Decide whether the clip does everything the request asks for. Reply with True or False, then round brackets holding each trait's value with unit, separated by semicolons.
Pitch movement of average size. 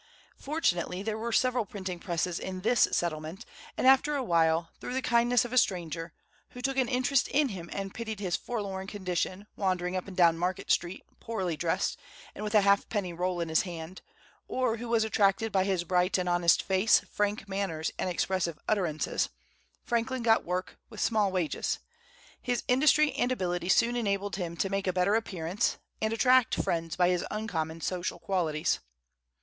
True (4.4 semitones)